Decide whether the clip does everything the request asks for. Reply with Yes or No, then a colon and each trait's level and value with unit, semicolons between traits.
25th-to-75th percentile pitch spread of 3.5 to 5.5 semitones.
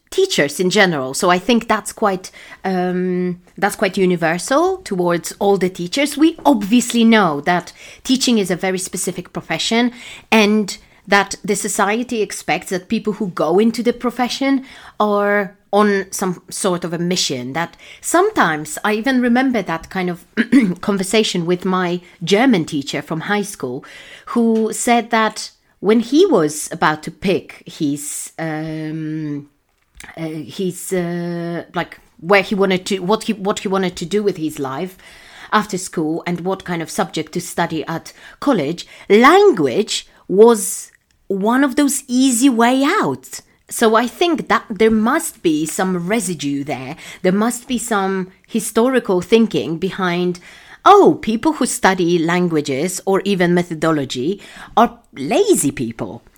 Yes: average, 4.5 semitones